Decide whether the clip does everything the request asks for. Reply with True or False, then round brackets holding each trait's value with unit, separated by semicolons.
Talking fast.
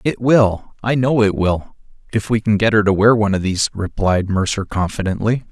False (195 wpm)